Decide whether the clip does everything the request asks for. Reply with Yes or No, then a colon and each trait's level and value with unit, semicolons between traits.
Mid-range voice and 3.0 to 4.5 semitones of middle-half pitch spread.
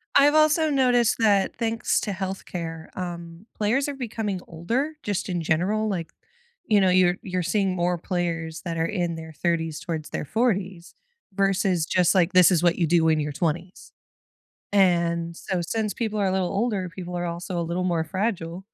Yes: medium, 180 Hz; average, 3.5 semitones